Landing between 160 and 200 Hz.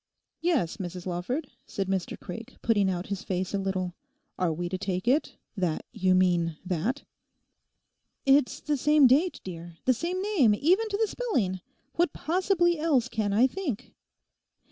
No: high, 220 Hz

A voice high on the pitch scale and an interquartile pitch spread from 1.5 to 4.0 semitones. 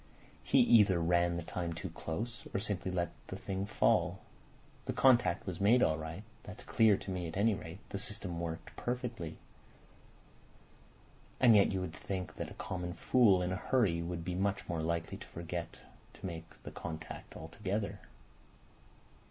No: very low, 90 Hz; average, 3.6 semitones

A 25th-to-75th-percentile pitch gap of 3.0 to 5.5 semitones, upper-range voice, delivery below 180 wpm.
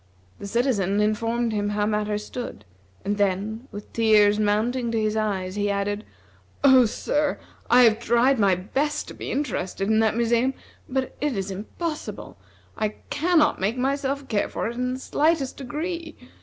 Yes: average, 4.2 semitones; high, 225 Hz; average, 165 wpm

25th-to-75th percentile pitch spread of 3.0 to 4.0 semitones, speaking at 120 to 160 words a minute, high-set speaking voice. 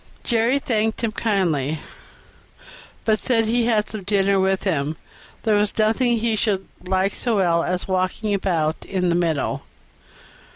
Yes: average, 3.4 semitones; average, 155 wpm; high, 200 Hz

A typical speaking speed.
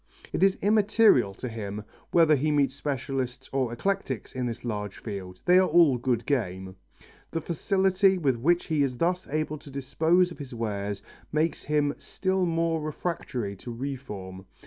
Yes: average, 165 wpm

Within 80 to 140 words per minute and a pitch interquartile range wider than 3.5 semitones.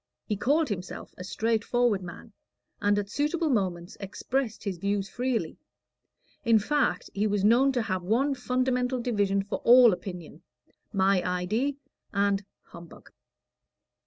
Yes: slow, 135 wpm; average, 4.2 semitones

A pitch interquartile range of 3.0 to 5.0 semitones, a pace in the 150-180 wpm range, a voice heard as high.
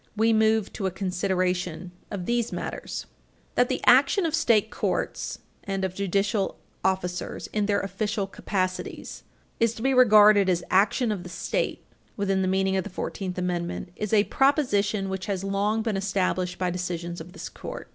No: narrow, 2.6 semitones; average, 170 wpm; high, 195 Hz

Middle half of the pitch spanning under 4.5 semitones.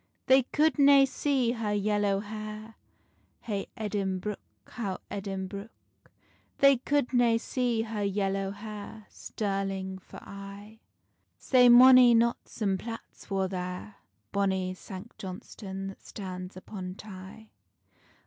Yes: average, 3.1 semitones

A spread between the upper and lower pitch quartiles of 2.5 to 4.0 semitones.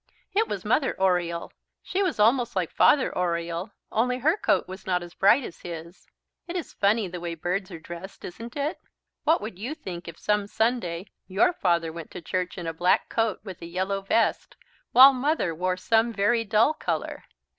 No: average, 5.3 semitones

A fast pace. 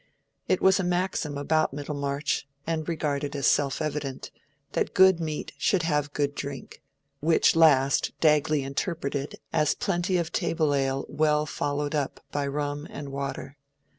No: average, 145 wpm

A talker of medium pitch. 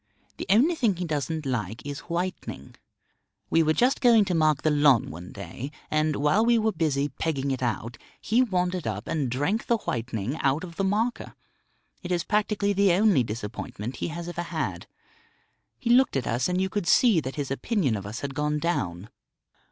Yes: medium, 155 Hz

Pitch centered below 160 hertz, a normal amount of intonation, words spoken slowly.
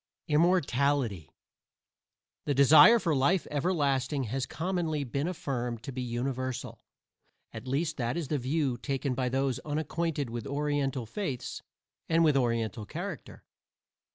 Yes: medium, 140 Hz; average, 3.6 semitones; slow, 125 wpm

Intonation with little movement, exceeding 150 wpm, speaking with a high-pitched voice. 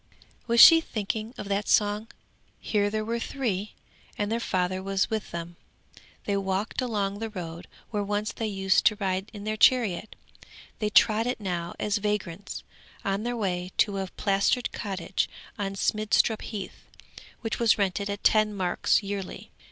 Yes: narrow, 2.0 semitones; average, 160 wpm; high, 205 Hz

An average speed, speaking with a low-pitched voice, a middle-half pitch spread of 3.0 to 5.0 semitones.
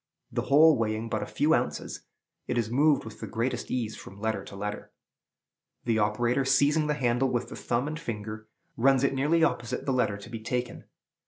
Yes: average, 195 wpm; low, 120 Hz; average, 3.7 semitones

